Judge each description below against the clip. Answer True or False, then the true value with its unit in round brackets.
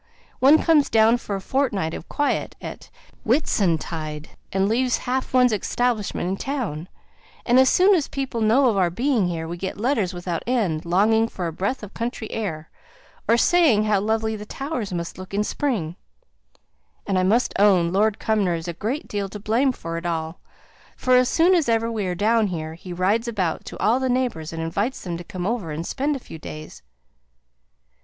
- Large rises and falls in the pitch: True (5.9 semitones)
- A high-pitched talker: True (210 Hz)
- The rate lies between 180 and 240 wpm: True (195 wpm)